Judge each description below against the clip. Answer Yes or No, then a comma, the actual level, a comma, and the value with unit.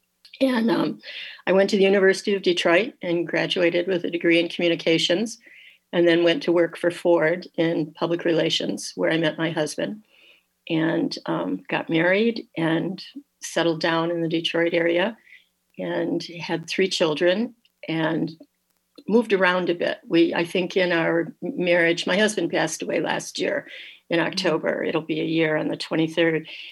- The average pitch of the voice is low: No, medium, 170 Hz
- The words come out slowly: No, average, 160 wpm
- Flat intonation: Yes, narrow, 2.2 semitones